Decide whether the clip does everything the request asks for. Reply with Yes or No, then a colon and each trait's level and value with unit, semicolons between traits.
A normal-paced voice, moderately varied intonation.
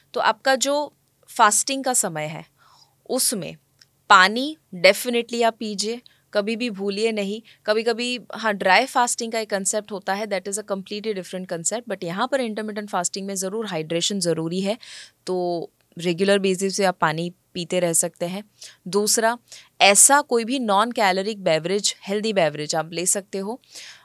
Yes: average, 160 wpm; average, 3.7 semitones